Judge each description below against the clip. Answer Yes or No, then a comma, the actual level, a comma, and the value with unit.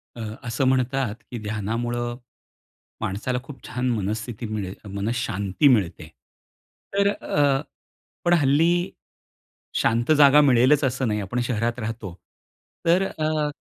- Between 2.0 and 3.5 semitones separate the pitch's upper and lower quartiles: No, average, 4.5 semitones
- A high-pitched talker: No, low, 120 Hz